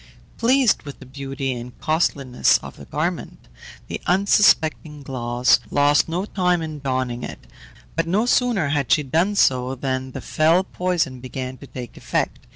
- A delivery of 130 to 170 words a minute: Yes, average, 160 wpm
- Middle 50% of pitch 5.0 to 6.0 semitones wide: Yes, average, 5.3 semitones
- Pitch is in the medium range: Yes, medium, 145 Hz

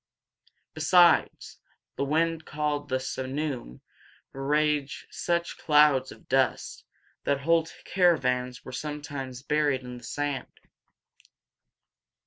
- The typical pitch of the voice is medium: Yes, medium, 145 Hz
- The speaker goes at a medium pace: No, slow, 100 wpm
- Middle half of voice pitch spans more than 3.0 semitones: No, narrow, 2.6 semitones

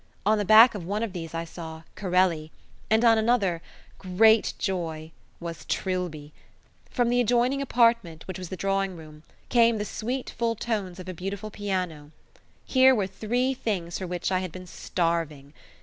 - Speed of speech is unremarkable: Yes, average, 170 wpm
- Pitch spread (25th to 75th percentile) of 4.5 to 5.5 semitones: Yes, average, 4.8 semitones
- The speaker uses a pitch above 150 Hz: Yes, high, 190 Hz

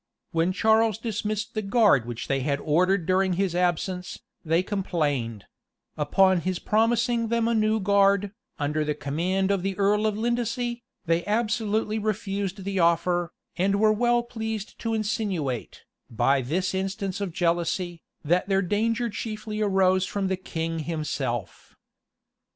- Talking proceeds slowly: No, average, 145 wpm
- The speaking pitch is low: No, high, 195 Hz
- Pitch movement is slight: No, average, 4.1 semitones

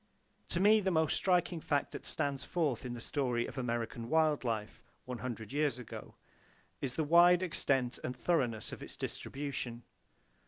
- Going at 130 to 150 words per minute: No, average, 165 wpm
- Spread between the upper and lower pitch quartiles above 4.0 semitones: Yes, average, 5.0 semitones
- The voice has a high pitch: No, medium, 140 Hz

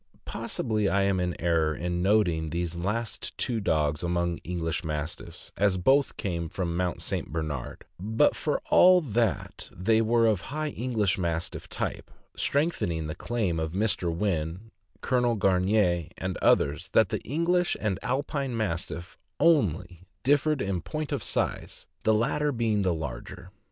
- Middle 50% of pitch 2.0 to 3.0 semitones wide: No, wide, 5.5 semitones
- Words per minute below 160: Yes, average, 150 wpm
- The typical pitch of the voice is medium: No, very low, 95 Hz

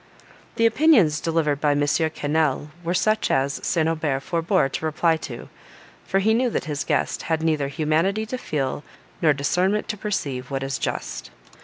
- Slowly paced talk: No, average, 170 wpm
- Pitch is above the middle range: No, medium, 160 Hz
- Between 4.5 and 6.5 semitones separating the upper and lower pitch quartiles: Yes, average, 4.8 semitones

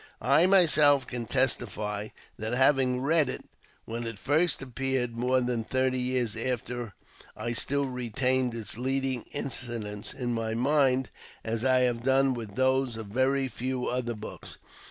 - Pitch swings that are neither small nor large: No, narrow, 2.3 semitones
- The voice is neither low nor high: No, low, 125 Hz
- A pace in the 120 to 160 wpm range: Yes, average, 150 wpm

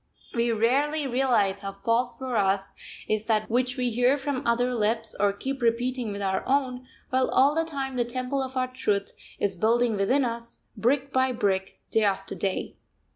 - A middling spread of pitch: Yes, average, 3.5 semitones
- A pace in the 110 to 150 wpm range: No, average, 180 wpm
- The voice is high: Yes, high, 240 Hz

